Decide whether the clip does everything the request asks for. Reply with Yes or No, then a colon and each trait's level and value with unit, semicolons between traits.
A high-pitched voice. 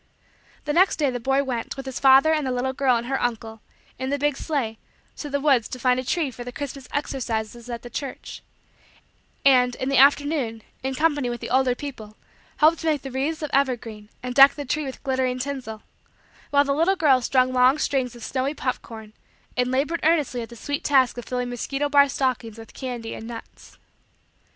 Yes: very high, 260 Hz